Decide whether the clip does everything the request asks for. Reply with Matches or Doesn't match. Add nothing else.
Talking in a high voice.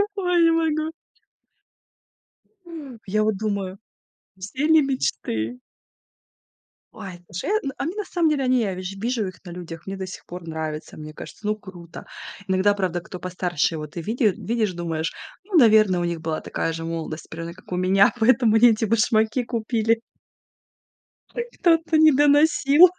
Matches